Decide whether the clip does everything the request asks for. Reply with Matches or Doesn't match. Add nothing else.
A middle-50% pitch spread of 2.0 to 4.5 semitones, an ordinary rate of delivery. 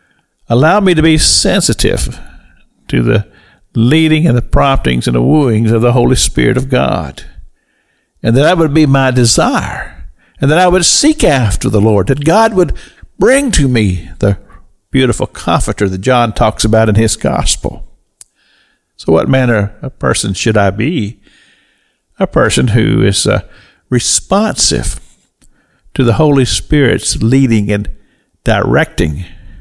Doesn't match